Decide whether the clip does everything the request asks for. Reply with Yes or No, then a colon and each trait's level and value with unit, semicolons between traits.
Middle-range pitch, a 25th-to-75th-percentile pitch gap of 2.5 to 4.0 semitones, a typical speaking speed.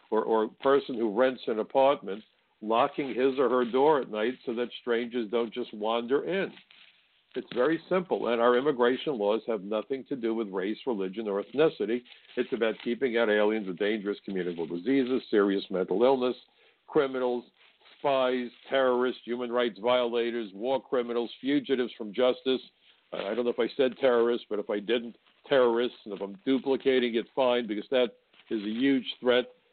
No: low, 120 Hz; average, 2.9 semitones; average, 170 wpm